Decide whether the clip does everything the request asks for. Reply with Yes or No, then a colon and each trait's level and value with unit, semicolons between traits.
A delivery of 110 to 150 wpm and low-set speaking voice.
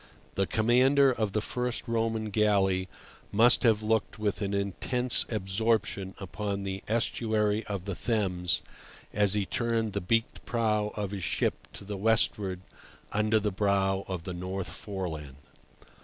Yes: average, 145 wpm; low, 105 Hz